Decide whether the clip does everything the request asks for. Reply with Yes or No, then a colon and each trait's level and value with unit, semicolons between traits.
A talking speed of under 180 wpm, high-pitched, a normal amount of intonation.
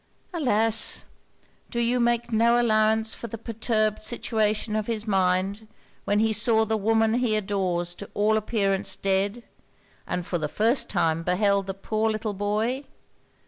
No: average, 150 wpm; high, 215 Hz; narrow, 2.2 semitones